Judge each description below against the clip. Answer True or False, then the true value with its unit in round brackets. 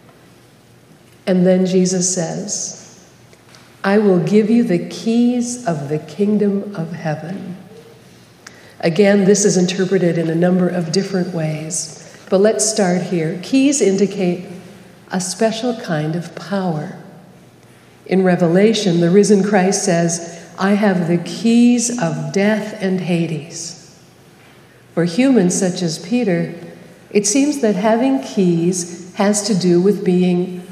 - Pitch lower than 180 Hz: False (185 Hz)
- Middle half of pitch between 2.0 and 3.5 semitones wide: True (2.9 semitones)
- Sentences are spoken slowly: True (125 wpm)